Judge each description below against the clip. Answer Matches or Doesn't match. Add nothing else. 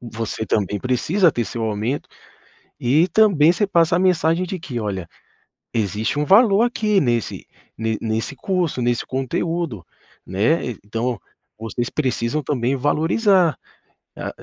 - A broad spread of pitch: Matches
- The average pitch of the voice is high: Doesn't match